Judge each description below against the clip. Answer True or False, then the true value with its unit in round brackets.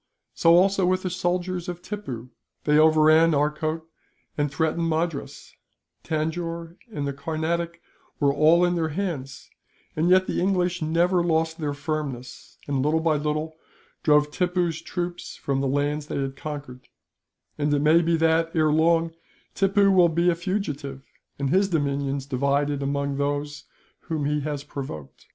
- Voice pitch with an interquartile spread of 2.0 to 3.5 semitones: True (3.1 semitones)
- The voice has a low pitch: False (155 Hz)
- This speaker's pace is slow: False (155 wpm)